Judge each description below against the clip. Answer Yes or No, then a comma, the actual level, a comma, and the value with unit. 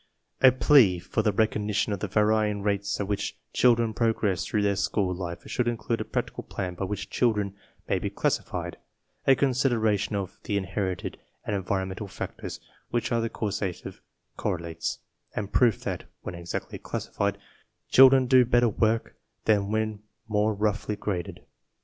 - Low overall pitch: Yes, low, 105 Hz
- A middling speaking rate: Yes, average, 155 wpm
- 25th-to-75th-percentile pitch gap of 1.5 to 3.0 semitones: Yes, narrow, 2.5 semitones